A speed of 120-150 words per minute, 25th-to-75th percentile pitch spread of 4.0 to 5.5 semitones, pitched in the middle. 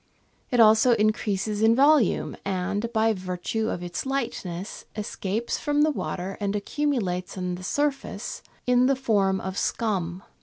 No: average, 145 wpm; average, 4.6 semitones; high, 215 Hz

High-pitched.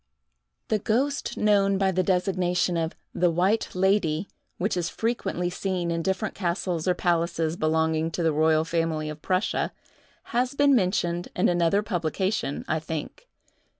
No: medium, 180 Hz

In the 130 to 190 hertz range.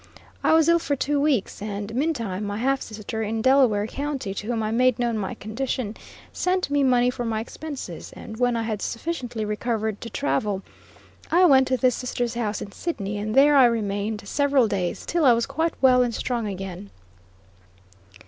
No: high, 235 Hz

